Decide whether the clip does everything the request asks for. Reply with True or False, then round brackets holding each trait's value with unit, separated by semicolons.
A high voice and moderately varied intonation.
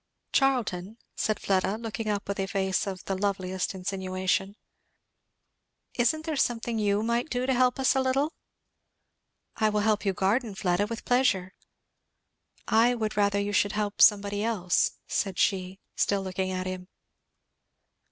True (205 Hz; 3.3 semitones)